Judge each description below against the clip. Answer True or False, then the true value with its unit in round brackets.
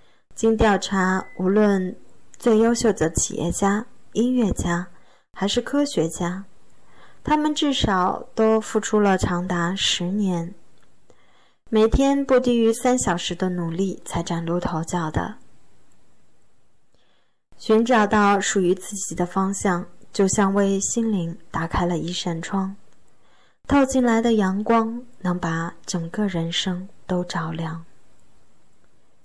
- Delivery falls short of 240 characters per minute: True (175 characters per minute)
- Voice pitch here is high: True (195 Hz)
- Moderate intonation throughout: True (4.1 semitones)